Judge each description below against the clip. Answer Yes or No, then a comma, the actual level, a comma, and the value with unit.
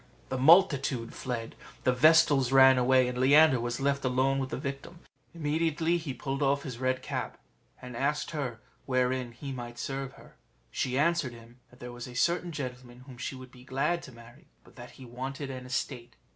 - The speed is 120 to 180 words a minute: No, average, 190 wpm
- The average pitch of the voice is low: Yes, low, 130 Hz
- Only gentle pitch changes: Yes, narrow, 2.2 semitones